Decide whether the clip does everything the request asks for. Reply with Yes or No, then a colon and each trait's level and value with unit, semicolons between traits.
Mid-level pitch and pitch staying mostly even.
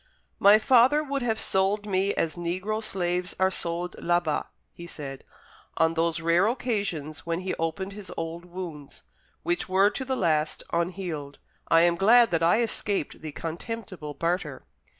No: medium, 180 Hz; average, 3.9 semitones